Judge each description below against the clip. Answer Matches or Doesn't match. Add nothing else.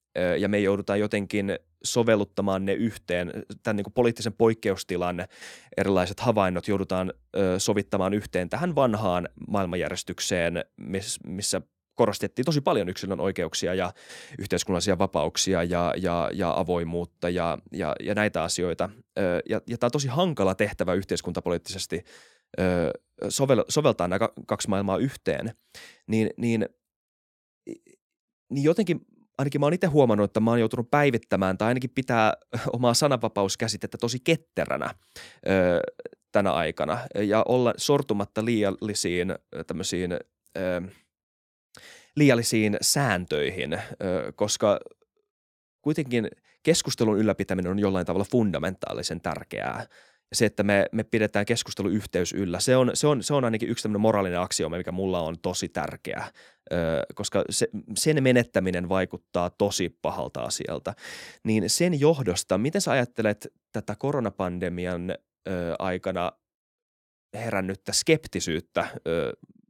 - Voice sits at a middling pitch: Doesn't match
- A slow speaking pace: Doesn't match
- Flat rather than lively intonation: Doesn't match